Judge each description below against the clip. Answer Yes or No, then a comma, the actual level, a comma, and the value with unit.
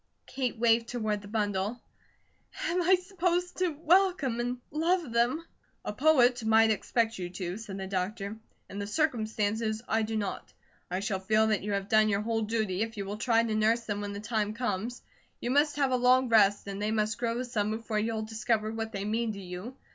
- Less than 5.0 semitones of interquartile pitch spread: Yes, average, 2.9 semitones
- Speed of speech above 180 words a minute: Yes, fast, 205 wpm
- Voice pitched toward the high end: Yes, high, 220 Hz